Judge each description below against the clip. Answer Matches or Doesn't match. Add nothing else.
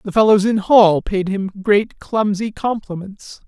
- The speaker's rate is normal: Matches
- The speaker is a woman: Doesn't match